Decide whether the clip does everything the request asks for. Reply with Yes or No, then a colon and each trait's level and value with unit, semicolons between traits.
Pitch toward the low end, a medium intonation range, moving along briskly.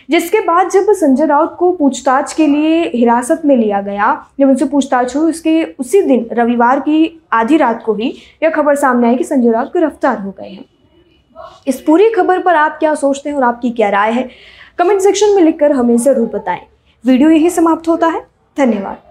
No: very high, 290 Hz; average, 4.9 semitones; fast, 200 wpm